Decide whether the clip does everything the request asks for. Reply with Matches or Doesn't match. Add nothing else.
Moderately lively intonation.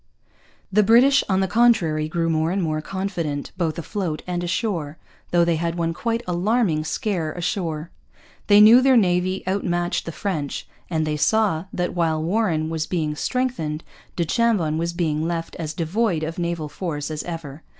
Matches